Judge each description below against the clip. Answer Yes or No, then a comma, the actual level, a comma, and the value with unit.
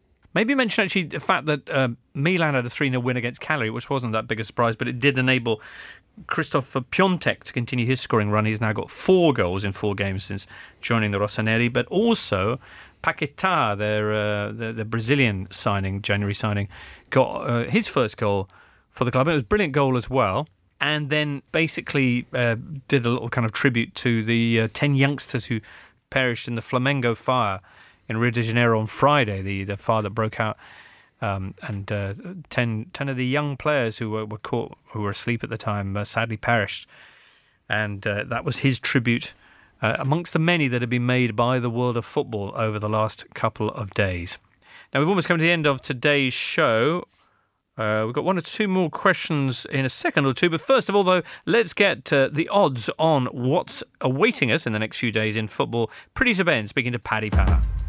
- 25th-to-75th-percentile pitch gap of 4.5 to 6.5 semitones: Yes, average, 4.8 semitones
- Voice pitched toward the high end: No, low, 120 Hz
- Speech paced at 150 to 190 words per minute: No, fast, 205 wpm